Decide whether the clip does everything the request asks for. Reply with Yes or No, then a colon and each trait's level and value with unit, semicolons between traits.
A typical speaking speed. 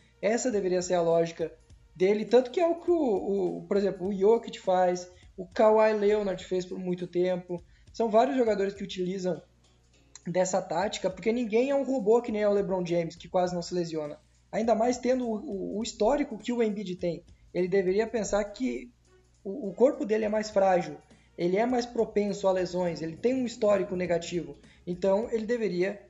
No: fast, 190 wpm